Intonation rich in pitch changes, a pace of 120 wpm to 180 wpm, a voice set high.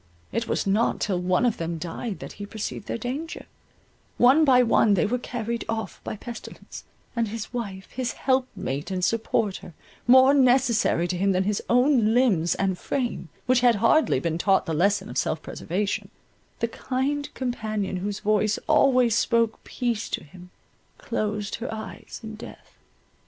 No: average, 4.2 semitones; average, 165 wpm; high, 220 Hz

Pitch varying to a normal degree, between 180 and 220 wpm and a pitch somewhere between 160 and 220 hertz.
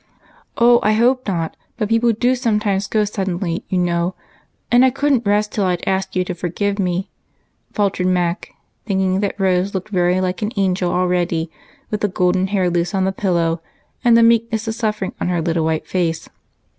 Yes: average, 3.1 semitones; average, 190 wpm; high, 190 Hz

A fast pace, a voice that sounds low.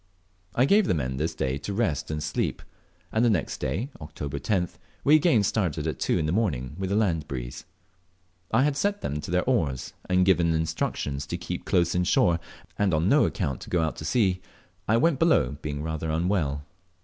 Yes: fast, 210 wpm; very low, 85 Hz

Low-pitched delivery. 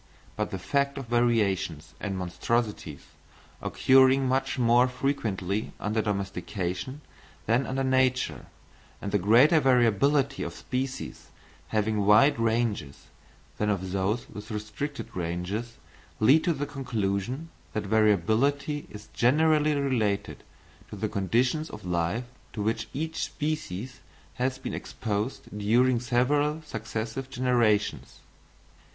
Yes: low, 115 Hz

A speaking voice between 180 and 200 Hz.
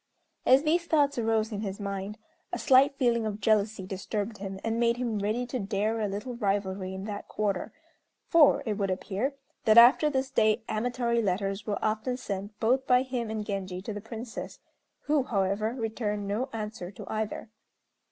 No: high, 220 Hz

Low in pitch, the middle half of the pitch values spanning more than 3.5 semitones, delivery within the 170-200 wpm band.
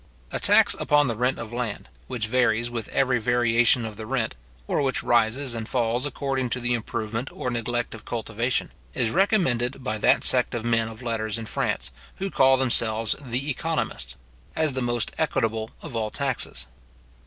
No: low, 120 Hz; narrow, 2.6 semitones; average, 175 wpm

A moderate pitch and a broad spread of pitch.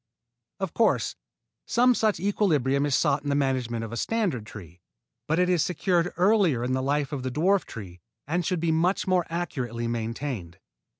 Yes: medium, 145 Hz; wide, 6.7 semitones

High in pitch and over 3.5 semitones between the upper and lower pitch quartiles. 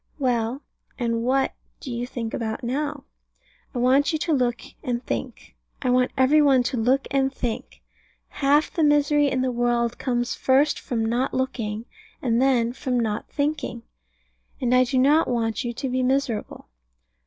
No: very high, 255 Hz; narrow, 2.4 semitones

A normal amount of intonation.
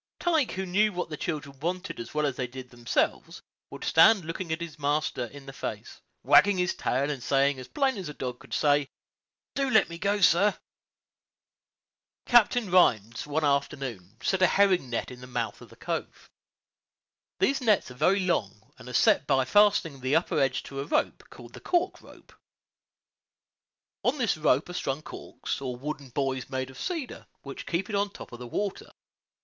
No: wide, 6.7 semitones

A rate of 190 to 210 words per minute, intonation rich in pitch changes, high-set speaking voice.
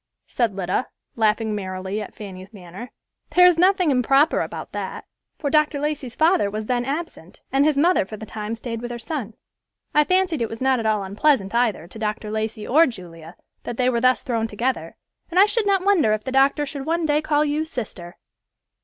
Yes: fast, 205 wpm; wide, 6.0 semitones; high, 245 Hz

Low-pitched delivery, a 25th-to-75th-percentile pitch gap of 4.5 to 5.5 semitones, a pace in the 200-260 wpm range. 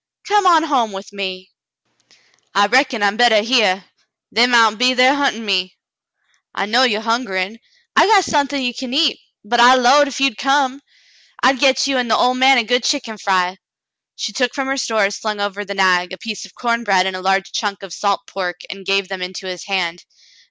No: high, 225 Hz; average, 4.8 semitones; fast, 205 wpm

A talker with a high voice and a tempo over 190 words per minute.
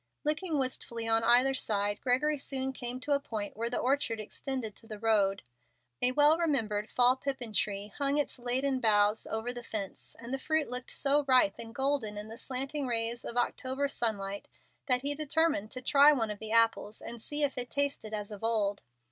Yes: high, 245 Hz; average, 200 wpm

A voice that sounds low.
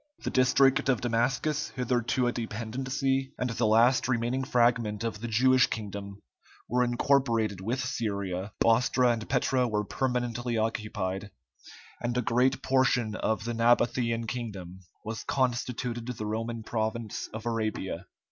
Yes: low, 120 Hz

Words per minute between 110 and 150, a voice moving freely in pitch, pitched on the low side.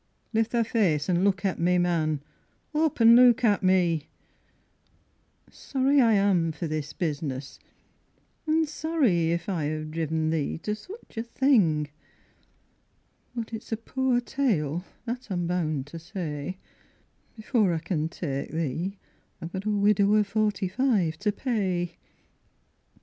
No: average, 140 wpm; wide, 5.8 semitones; medium, 185 Hz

